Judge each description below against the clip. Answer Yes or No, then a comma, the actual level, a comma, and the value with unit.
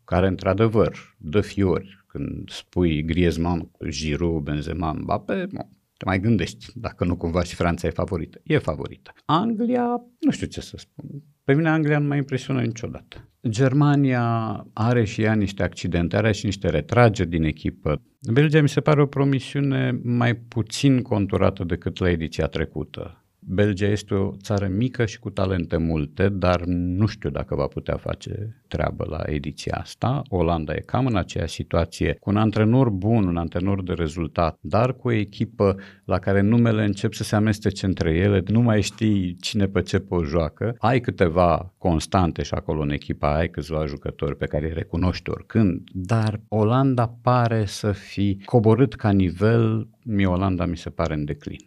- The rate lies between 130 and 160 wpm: No, fast, 170 wpm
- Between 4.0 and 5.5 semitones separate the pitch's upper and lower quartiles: Yes, average, 5.1 semitones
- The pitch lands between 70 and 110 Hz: Yes, low, 100 Hz